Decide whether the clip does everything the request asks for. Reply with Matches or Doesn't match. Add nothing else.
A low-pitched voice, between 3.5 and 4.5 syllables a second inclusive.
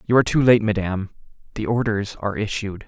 Doesn't match